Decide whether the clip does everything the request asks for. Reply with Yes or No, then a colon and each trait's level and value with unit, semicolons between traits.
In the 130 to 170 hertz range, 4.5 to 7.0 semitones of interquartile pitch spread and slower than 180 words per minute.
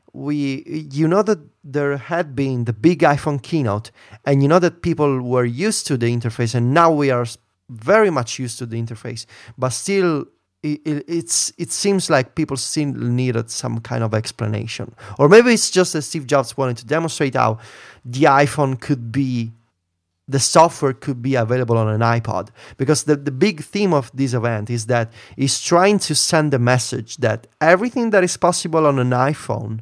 No: low, 135 Hz; average, 5.0 semitones; average, 185 wpm